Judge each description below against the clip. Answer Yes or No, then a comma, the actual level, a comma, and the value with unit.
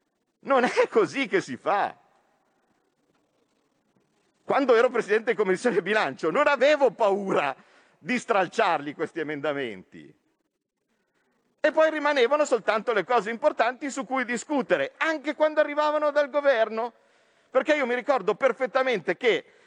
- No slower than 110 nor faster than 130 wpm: Yes, average, 125 wpm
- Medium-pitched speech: No, very high, 280 Hz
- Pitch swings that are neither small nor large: Yes, average, 4.3 semitones